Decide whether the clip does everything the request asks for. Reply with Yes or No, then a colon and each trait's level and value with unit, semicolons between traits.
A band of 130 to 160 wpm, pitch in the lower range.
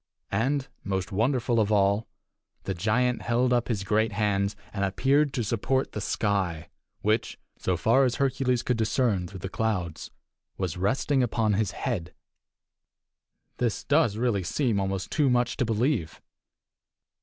Yes: average, 145 wpm; low, 110 Hz